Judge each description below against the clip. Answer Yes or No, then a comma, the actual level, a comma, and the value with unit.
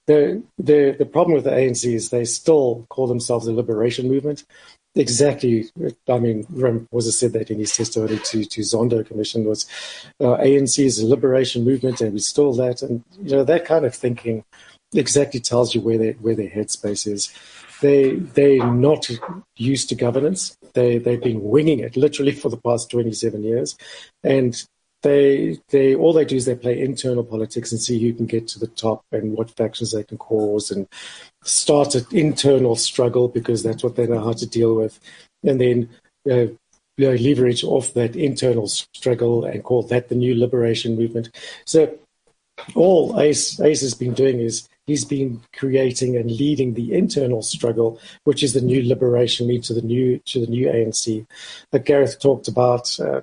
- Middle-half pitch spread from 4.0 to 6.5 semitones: No, average, 2.8 semitones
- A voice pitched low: Yes, low, 120 Hz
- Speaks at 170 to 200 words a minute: Yes, average, 185 wpm